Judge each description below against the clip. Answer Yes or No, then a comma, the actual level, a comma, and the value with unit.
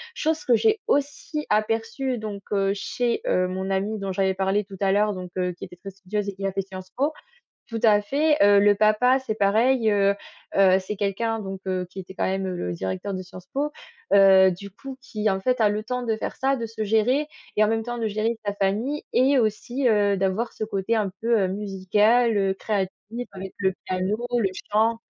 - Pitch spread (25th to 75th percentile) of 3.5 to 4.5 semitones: No, average, 3.1 semitones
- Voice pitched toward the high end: Yes, high, 205 Hz